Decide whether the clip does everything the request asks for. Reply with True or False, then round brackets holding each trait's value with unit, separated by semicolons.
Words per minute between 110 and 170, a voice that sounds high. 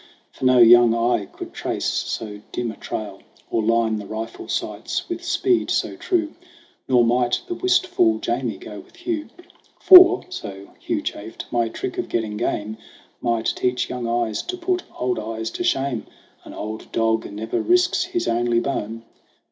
False (165 wpm; 120 Hz)